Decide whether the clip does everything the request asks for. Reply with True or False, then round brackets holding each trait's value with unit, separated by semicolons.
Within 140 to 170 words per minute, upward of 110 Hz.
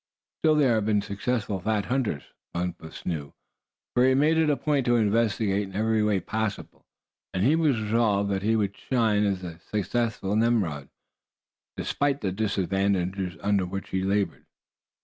False (165 wpm; 105 Hz)